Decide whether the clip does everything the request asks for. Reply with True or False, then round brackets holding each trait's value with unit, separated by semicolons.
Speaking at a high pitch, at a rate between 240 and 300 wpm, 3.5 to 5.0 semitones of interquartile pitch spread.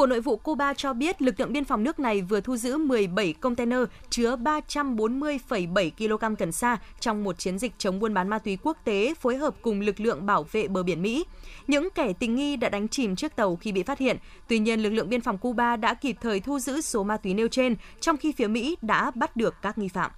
True (235 Hz; 245 wpm; 4.7 semitones)